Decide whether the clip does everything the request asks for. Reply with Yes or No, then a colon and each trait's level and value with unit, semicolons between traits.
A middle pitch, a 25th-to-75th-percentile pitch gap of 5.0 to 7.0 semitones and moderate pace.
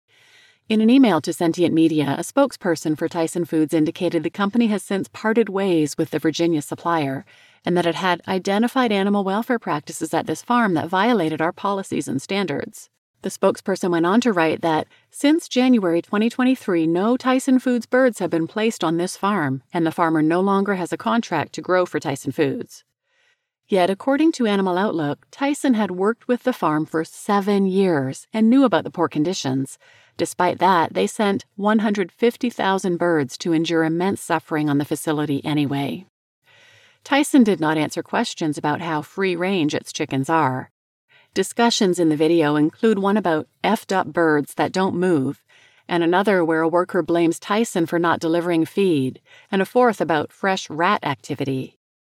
Yes: medium, 175 Hz; wide, 5.4 semitones; average, 170 wpm